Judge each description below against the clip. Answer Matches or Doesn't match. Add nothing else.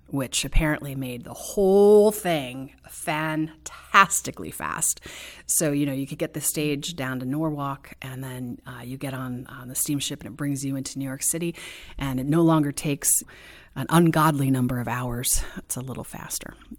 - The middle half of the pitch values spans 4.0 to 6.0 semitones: Doesn't match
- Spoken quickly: Doesn't match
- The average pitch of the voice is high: Doesn't match